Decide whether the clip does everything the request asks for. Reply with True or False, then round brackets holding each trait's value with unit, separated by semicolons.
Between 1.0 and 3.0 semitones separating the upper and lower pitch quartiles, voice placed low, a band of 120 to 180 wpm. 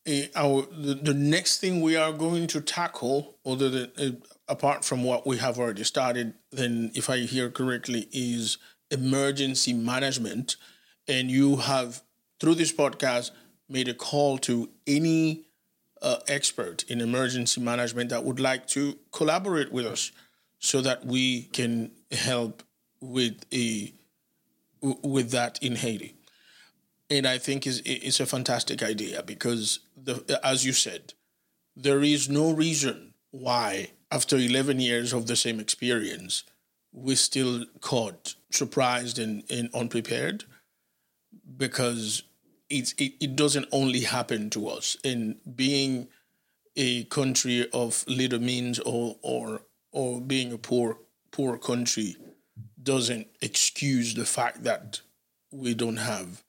True (2.5 semitones; 130 Hz; 135 wpm)